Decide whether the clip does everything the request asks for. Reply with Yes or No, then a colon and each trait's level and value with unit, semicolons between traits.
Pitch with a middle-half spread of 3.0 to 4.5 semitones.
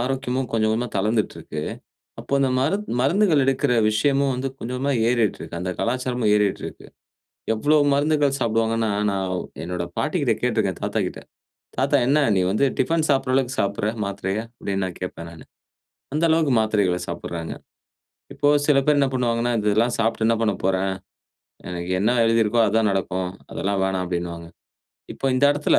No: wide, 5.5 semitones